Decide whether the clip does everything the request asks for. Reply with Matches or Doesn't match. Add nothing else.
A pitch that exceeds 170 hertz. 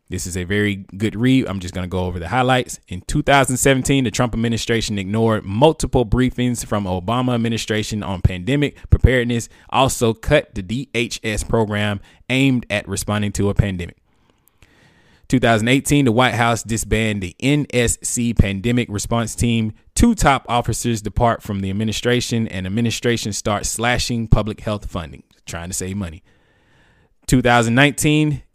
Doesn't match